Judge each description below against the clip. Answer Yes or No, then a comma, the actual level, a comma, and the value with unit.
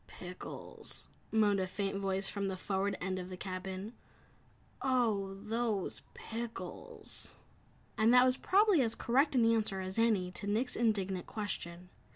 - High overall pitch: Yes, high, 205 Hz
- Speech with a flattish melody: No, average, 3.4 semitones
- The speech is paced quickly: No, average, 145 wpm